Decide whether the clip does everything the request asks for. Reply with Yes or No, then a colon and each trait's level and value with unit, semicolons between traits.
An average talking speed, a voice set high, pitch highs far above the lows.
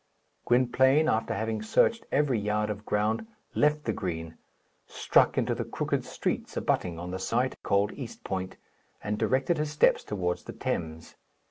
No: average, 155 wpm; low, 105 Hz; wide, 5.7 semitones